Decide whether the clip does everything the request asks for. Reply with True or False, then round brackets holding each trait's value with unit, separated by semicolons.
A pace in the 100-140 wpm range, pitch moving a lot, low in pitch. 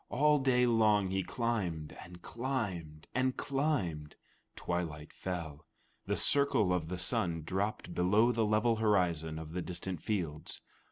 True (135 wpm; 5.7 semitones; 95 Hz)